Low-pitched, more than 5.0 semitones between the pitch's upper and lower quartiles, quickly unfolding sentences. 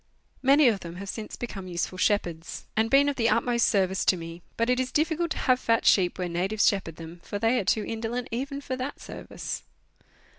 No: high, 225 Hz; wide, 5.5 semitones; fast, 215 wpm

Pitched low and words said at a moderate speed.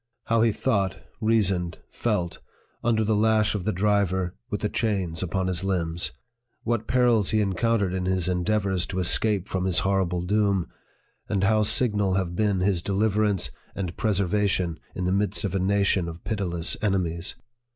Yes: very low, 95 Hz; average, 160 wpm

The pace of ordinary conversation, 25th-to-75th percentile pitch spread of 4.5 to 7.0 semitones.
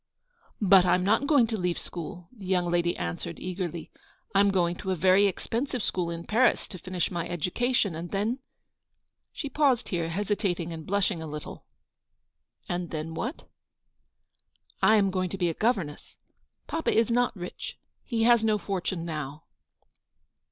No: average, 175 wpm; average, 4.1 semitones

